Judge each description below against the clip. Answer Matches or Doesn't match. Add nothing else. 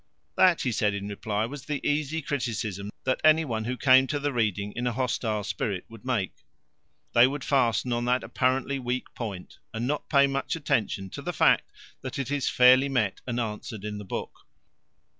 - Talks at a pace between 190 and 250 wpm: Matches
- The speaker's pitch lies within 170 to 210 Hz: Doesn't match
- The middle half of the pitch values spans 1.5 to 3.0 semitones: Doesn't match